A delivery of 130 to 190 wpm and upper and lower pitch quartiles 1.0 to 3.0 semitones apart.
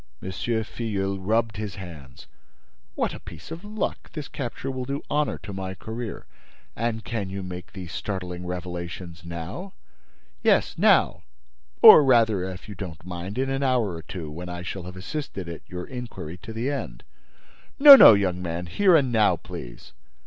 No: average, 170 wpm; average, 5.2 semitones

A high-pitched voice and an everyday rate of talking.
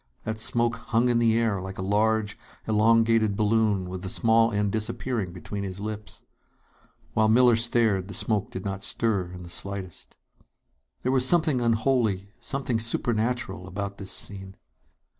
No: low, 110 Hz; average, 155 wpm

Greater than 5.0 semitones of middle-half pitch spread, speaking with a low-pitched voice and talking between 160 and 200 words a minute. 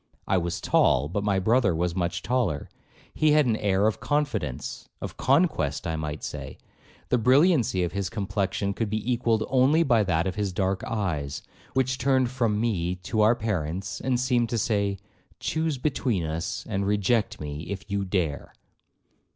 Yes: wide, 5.4 semitones; low, 105 Hz; average, 170 wpm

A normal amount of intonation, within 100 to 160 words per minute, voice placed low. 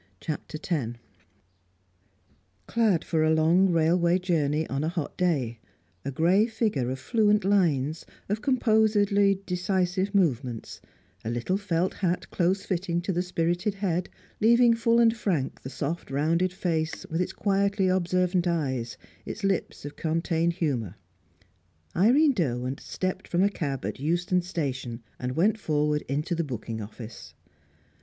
No: average, 4.9 semitones; average, 140 wpm; medium, 175 Hz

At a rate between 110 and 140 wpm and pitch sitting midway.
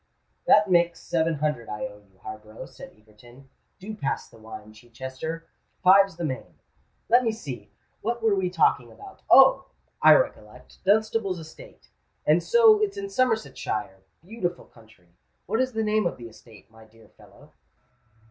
No: average, 150 wpm; medium, 165 Hz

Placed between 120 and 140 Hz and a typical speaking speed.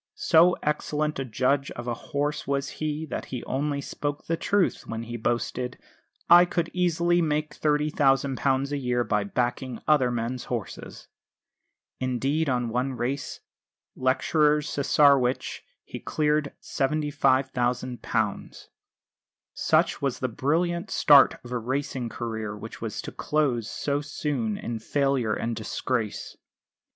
No: low, 135 Hz; slow, 130 wpm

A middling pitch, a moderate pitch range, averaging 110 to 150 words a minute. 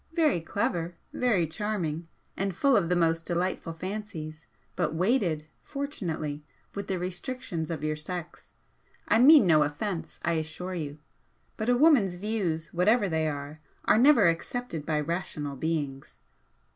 Yes: medium, 175 Hz; average, 4.9 semitones; average, 145 wpm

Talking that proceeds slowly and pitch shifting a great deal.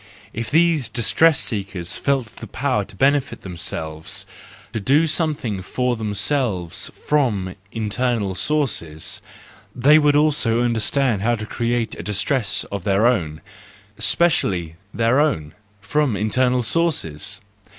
Yes: slow, 120 wpm; wide, 5.9 semitones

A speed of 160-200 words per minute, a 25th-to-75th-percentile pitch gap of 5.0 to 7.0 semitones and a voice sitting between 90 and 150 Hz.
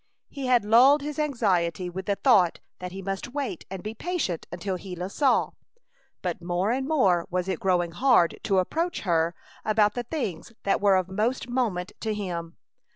No: average, 180 wpm; wide, 5.6 semitones; high, 195 Hz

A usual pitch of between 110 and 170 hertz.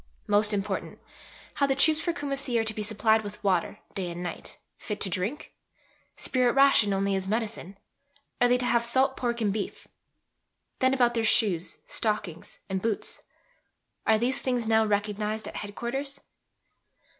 No: high, 220 Hz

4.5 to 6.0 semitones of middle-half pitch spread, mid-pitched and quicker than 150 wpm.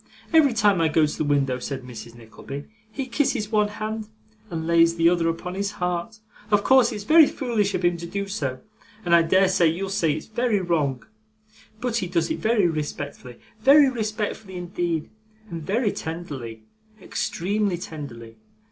Yes: average, 5.0 semitones; medium, 180 Hz; average, 175 wpm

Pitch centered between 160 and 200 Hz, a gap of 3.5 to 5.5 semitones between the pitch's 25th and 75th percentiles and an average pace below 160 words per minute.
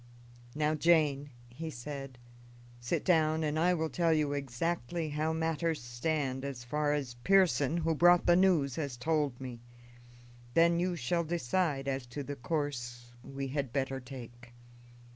No: medium, 145 Hz; average, 3.8 semitones; average, 150 wpm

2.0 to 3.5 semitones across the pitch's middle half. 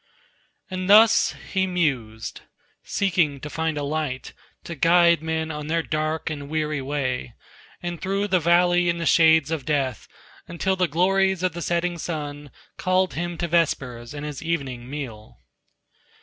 Yes: average, 3.2 semitones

